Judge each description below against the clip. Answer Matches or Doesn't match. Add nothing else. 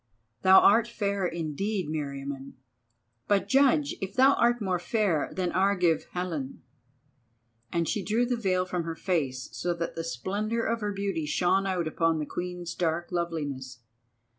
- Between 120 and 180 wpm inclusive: Matches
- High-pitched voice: Doesn't match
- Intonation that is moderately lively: Matches